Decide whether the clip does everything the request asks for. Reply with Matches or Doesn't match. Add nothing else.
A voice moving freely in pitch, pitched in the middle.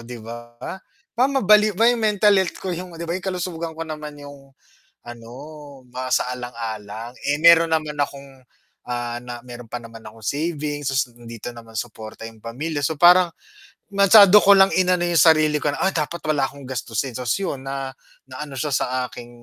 Matches